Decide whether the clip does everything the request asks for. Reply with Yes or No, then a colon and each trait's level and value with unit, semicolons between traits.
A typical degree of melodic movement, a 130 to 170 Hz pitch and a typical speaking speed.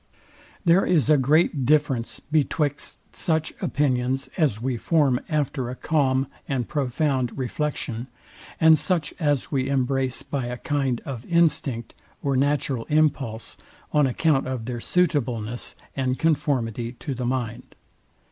No: average, 3.3 semitones; low, 135 Hz; slow, 130 wpm